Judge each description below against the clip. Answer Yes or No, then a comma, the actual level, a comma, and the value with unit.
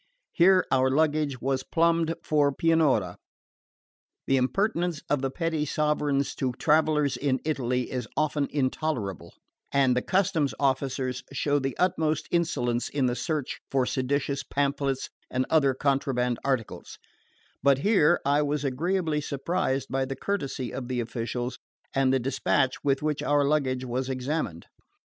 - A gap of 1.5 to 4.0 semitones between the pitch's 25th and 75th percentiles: Yes, average, 2.9 semitones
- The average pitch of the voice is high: No, medium, 140 Hz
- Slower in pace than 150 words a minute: Yes, average, 140 wpm